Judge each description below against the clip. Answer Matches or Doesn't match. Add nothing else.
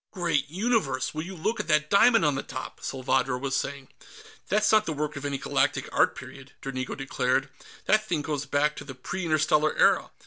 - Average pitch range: Matches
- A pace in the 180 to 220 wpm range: Matches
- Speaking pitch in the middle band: Matches